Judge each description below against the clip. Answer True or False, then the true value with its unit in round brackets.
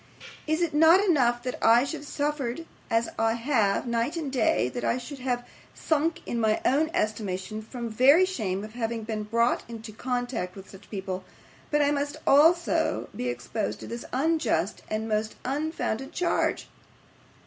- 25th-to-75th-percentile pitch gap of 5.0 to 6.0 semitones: True (5.3 semitones)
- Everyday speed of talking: True (170 wpm)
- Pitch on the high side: True (240 Hz)